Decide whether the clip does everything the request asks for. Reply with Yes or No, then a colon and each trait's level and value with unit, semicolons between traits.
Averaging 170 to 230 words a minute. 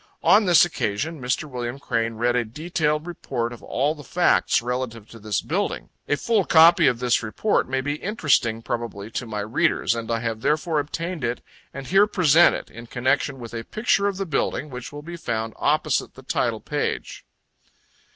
Yes: average, 190 wpm